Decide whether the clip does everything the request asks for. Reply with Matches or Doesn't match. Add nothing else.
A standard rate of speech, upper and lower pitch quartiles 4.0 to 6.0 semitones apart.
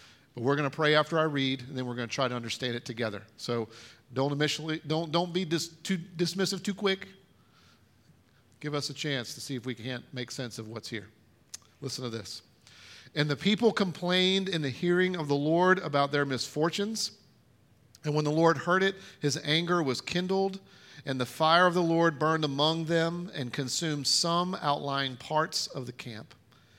Matches